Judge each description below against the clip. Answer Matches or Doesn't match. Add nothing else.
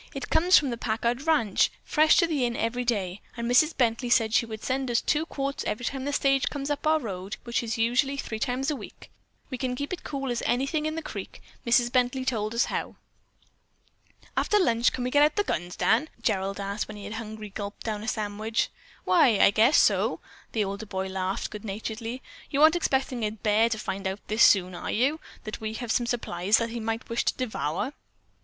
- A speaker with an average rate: Doesn't match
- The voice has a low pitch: Doesn't match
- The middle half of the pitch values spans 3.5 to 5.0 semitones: Matches